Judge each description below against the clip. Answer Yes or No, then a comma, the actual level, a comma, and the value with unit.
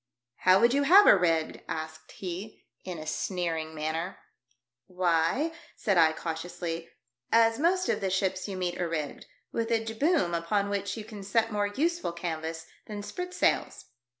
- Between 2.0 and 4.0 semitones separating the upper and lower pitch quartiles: No, wide, 5.4 semitones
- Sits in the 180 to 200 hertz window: Yes, medium, 185 Hz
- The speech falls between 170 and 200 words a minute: Yes, average, 180 wpm